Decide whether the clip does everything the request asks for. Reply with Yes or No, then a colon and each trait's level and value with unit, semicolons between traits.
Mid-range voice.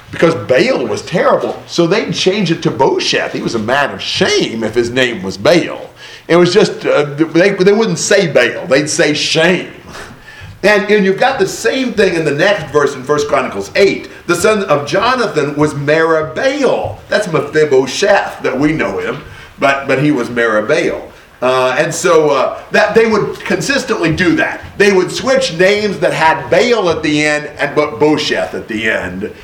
Yes: medium, 160 Hz